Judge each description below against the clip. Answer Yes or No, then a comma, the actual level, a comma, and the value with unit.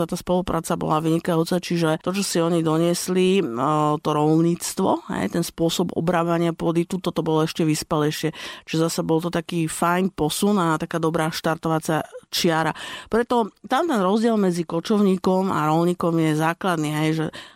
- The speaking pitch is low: No, medium, 170 Hz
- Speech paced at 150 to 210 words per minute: Yes, average, 160 wpm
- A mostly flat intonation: Yes, narrow, 2.2 semitones